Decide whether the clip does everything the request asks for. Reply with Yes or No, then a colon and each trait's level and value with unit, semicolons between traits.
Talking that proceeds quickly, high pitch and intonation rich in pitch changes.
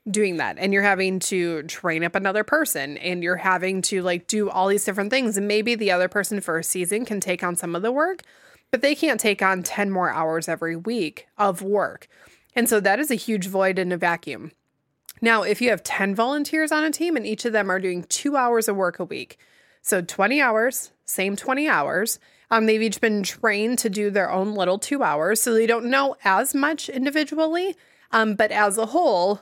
No: fast, 220 wpm; high, 205 Hz; average, 4.3 semitones